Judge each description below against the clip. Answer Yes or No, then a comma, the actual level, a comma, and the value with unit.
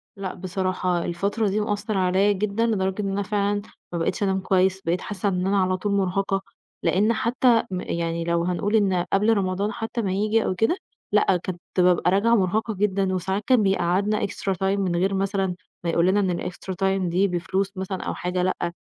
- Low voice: No, high, 195 Hz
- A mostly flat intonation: Yes, narrow, 2.0 semitones